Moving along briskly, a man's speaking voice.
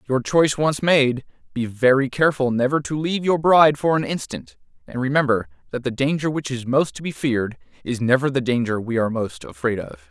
Yes: fast, 210 wpm; male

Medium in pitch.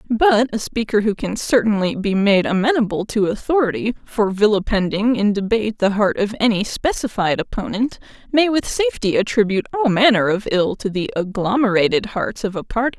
No: high, 215 Hz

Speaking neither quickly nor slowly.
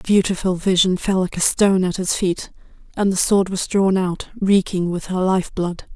No: fast, 210 wpm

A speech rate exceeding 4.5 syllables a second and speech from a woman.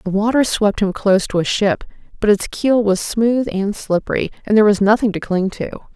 Yes: 5.5 syllables/s; female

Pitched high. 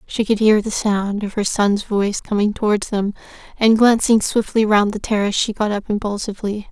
Yes: high, 210 Hz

